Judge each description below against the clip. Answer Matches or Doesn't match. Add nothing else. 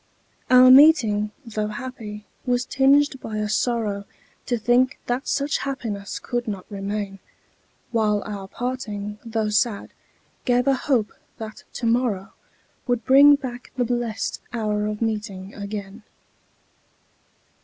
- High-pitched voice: Matches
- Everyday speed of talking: Doesn't match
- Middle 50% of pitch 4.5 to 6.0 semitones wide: Doesn't match